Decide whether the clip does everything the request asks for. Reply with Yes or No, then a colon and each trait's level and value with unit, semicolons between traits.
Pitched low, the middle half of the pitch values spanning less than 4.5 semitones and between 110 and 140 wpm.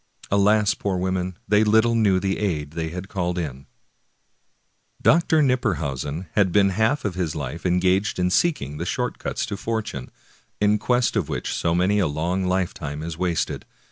No: very low, 95 Hz; average, 3.9 semitones; average, 165 wpm